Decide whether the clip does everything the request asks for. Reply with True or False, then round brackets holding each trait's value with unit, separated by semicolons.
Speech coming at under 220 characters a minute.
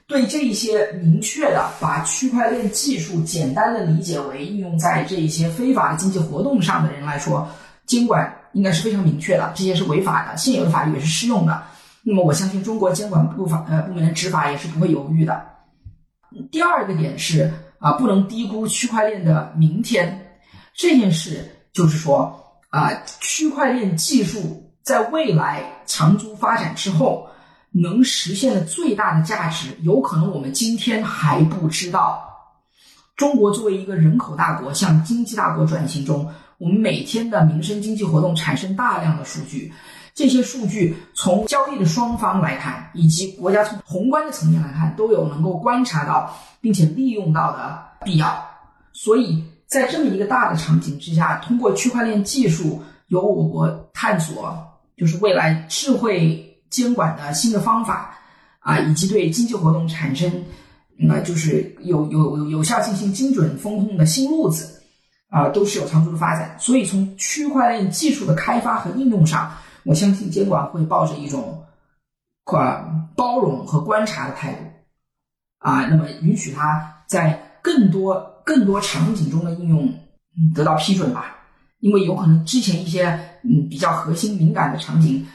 False (260 characters per minute)